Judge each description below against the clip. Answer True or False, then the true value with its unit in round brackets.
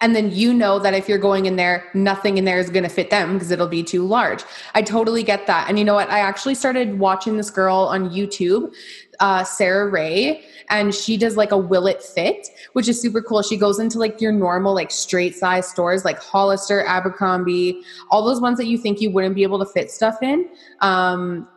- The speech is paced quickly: True (230 wpm)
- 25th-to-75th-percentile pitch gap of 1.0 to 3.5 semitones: True (2.9 semitones)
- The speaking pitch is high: True (200 Hz)